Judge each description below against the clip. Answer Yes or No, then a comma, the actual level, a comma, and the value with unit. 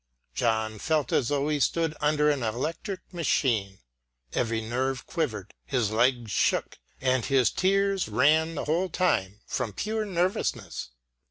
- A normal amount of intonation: No, wide, 6.4 semitones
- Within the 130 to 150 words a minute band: Yes, average, 140 wpm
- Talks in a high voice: No, medium, 140 Hz